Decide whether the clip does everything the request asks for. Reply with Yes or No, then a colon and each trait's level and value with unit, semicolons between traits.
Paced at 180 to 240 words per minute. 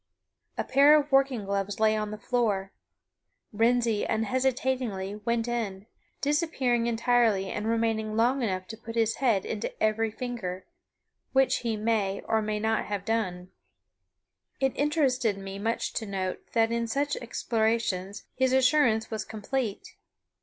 No: average, 140 wpm